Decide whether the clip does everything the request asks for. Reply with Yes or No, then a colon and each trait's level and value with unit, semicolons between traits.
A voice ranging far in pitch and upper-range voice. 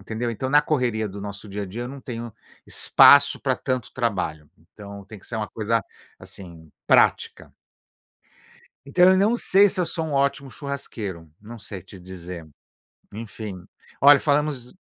No: wide, 5.8 semitones; low, 115 Hz